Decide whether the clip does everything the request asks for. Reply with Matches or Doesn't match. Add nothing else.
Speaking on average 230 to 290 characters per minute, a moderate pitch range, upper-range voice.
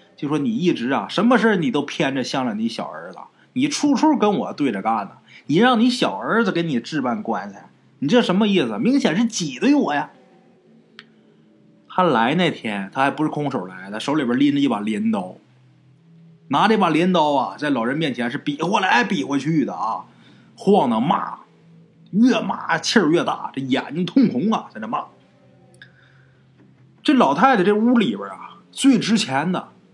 Doesn't match